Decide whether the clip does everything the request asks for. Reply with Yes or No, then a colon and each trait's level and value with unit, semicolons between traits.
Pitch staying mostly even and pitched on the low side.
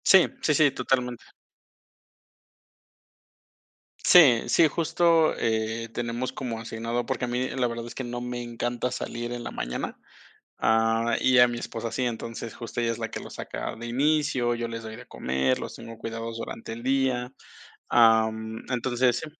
Yes: narrow, 1.7 semitones; low, 120 Hz